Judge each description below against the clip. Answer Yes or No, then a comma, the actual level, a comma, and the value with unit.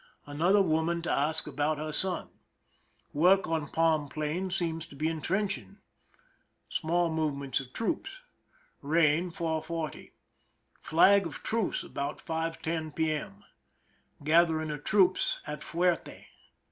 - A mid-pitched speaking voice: Yes, medium, 160 Hz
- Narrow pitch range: Yes, narrow, 2.3 semitones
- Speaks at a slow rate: Yes, slow, 120 wpm